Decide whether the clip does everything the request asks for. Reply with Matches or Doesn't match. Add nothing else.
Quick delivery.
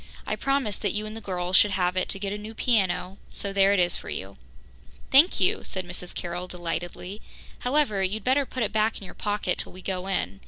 Matches